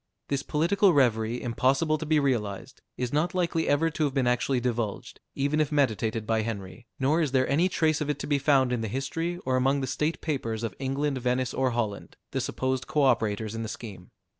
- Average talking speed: No, fast, 215 wpm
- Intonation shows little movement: No, average, 4.2 semitones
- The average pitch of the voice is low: Yes, low, 130 Hz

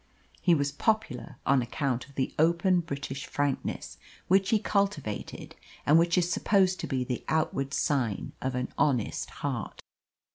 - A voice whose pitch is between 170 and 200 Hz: No, medium, 145 Hz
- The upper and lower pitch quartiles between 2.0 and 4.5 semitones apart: No, average, 5.2 semitones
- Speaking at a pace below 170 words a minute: Yes, average, 150 wpm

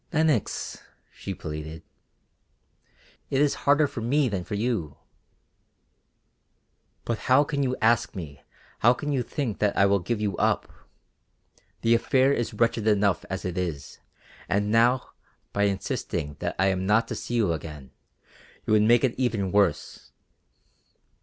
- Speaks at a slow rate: No, average, 150 wpm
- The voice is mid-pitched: No, low, 105 Hz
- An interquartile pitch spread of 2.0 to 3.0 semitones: No, average, 4.7 semitones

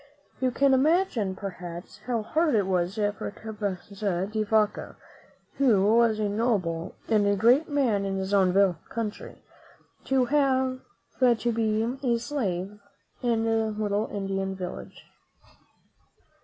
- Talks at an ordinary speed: No, slow, 130 wpm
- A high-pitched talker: Yes, high, 215 Hz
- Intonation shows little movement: No, average, 3.6 semitones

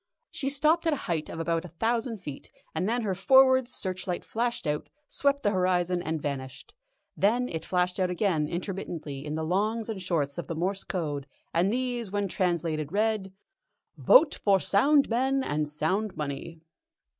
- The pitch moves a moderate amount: No, wide, 5.9 semitones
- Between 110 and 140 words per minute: No, average, 170 wpm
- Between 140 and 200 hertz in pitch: Yes, medium, 185 Hz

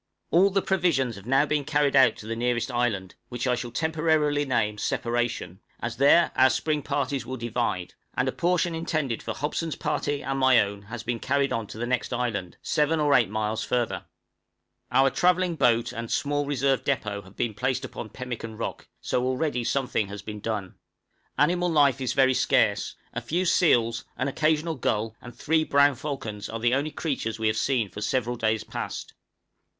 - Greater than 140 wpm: Yes, average, 190 wpm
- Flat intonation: No, average, 4.3 semitones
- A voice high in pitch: No, low, 130 Hz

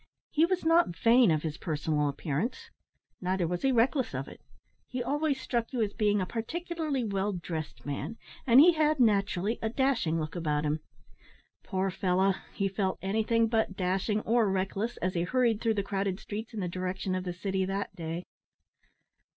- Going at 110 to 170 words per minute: No, average, 180 wpm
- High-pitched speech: Yes, high, 200 Hz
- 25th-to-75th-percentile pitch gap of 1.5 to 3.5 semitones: No, average, 4.7 semitones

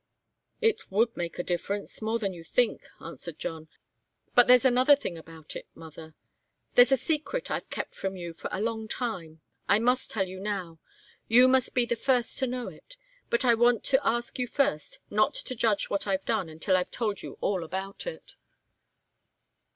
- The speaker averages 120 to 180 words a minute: No, average, 190 wpm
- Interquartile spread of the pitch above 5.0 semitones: Yes, wide, 5.5 semitones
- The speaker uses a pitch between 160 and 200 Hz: No, high, 220 Hz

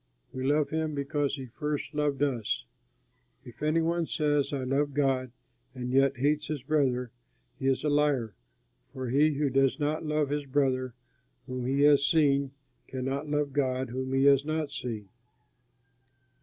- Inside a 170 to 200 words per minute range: No, average, 160 wpm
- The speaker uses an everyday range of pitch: No, narrow, 2.3 semitones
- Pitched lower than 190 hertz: Yes, medium, 140 Hz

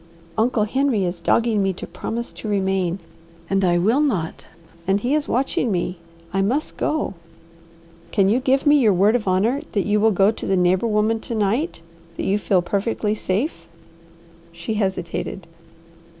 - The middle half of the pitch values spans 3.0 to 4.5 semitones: Yes, average, 3.9 semitones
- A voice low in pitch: No, high, 205 Hz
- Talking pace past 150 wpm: Yes, average, 175 wpm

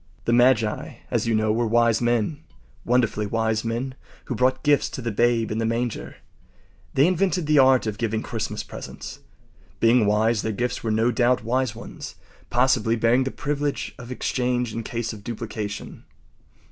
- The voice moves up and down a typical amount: No, narrow, 2.3 semitones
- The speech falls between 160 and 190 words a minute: Yes, average, 165 wpm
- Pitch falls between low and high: No, low, 120 Hz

